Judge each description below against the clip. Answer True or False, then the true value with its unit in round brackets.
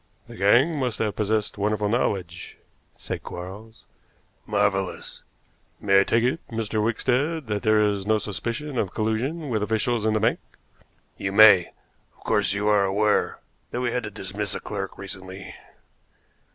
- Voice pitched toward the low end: True (105 Hz)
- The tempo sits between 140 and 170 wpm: True (155 wpm)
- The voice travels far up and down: False (2.6 semitones)